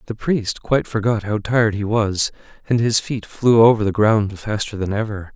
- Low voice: Yes, low, 110 Hz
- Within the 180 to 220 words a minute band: Yes, average, 200 wpm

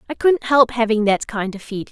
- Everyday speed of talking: No, fast, 250 wpm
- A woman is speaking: Yes, female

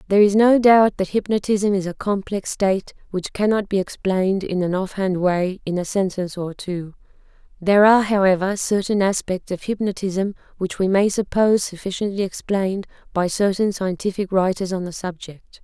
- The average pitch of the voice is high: Yes, high, 195 Hz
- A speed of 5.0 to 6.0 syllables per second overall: Yes, 5.3 syllables/s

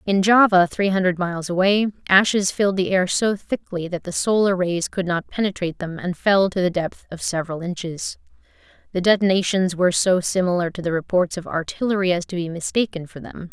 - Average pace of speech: Yes, average, 195 wpm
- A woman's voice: Yes, female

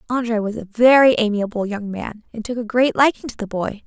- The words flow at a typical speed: No, fast, 235 wpm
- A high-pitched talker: Yes, high, 225 Hz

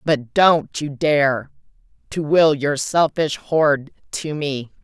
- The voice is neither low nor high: Yes, medium, 145 Hz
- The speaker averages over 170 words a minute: No, slow, 135 wpm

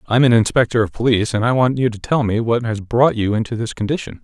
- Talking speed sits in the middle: No, fast, 270 wpm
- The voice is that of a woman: No, male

